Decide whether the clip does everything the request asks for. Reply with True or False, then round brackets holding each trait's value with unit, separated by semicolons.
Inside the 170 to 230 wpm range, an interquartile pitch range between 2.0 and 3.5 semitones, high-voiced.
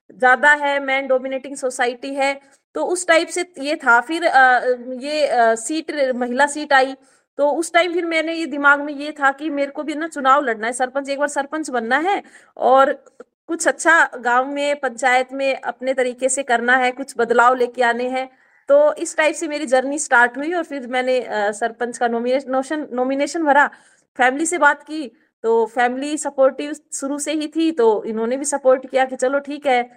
True (190 wpm; 2.7 semitones; 275 Hz)